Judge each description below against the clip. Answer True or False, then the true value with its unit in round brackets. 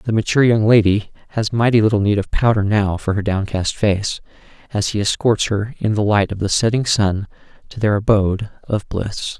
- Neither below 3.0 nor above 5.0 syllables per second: False (5.2 syllables/s)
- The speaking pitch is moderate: False (105 Hz)